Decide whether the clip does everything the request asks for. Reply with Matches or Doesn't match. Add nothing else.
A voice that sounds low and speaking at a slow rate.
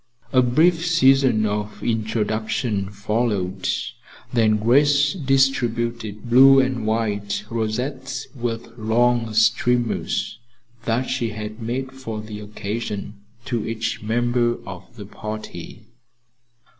Matches